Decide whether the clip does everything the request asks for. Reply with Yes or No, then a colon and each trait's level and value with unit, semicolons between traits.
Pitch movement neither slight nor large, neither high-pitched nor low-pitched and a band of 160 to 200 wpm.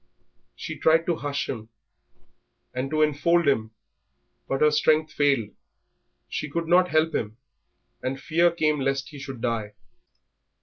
No: average, 3.1 semitones; medium, 145 Hz; average, 140 wpm